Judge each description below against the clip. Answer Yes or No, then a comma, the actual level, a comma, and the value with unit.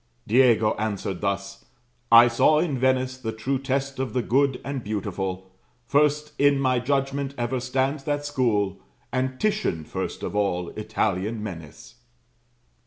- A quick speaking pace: No, average, 145 wpm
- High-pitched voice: No, low, 125 Hz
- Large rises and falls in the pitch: No, average, 4.6 semitones